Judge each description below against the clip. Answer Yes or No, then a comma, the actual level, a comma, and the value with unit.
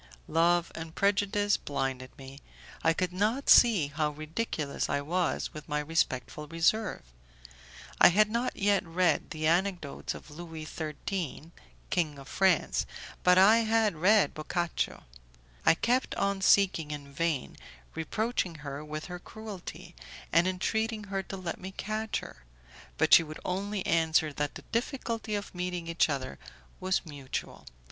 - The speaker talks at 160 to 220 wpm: No, average, 145 wpm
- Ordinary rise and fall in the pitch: Yes, average, 4.7 semitones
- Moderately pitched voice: Yes, medium, 175 Hz